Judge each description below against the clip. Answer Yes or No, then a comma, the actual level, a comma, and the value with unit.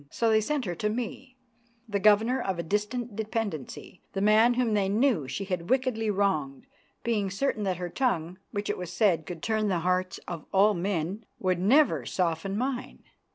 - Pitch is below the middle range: No, high, 205 Hz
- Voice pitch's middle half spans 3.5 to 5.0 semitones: Yes, average, 3.9 semitones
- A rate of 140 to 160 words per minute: No, average, 185 wpm